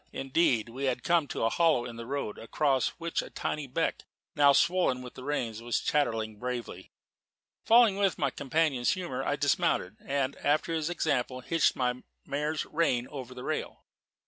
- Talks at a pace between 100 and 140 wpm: No, average, 175 wpm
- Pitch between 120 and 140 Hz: Yes, low, 135 Hz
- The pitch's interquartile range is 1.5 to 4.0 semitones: No, average, 4.4 semitones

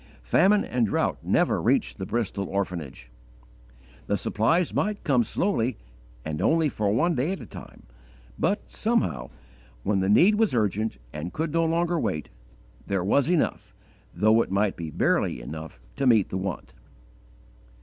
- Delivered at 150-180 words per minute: Yes, average, 155 wpm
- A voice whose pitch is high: No, low, 110 Hz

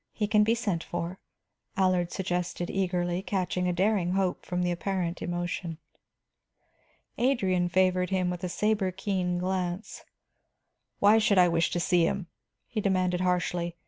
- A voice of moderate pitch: Yes, medium, 180 Hz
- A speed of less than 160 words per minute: Yes, average, 145 wpm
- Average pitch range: No, narrow, 1.7 semitones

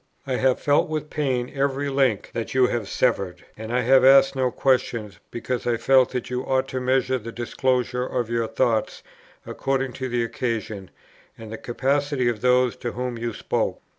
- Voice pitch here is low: Yes, low, 125 Hz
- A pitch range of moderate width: No, narrow, 2.1 semitones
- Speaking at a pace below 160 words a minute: No, average, 185 wpm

